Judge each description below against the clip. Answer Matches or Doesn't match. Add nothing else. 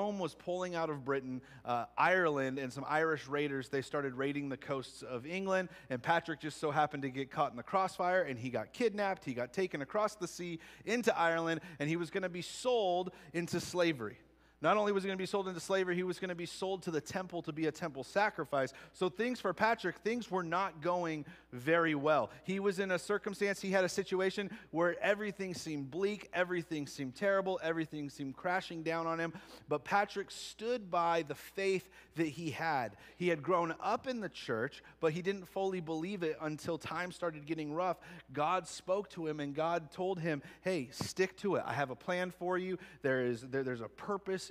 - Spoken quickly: Matches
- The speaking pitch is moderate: Matches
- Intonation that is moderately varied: Matches